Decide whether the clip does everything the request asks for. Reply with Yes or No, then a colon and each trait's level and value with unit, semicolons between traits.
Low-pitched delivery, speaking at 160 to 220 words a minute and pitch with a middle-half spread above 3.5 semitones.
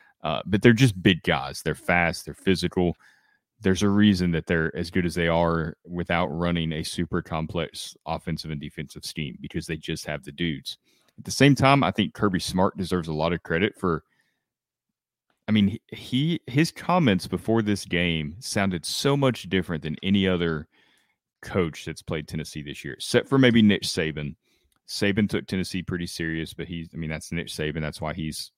Yes: very low, 85 Hz; average, 190 wpm; average, 4.1 semitones